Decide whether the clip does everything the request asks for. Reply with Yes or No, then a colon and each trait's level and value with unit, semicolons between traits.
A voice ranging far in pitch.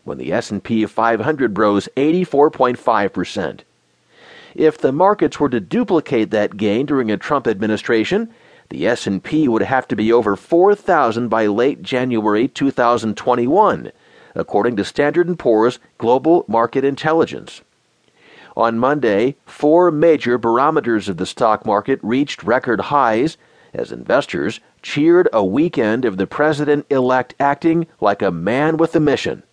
Yes: wide, 6.1 semitones